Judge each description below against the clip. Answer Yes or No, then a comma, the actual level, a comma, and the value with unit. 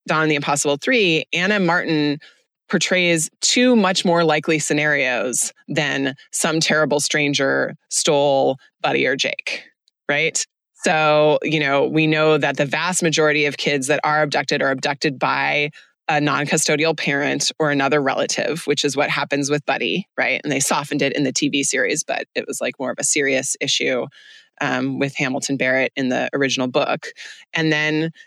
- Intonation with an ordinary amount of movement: No, narrow, 2.0 semitones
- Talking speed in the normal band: Yes, average, 165 wpm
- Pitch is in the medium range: Yes, medium, 150 Hz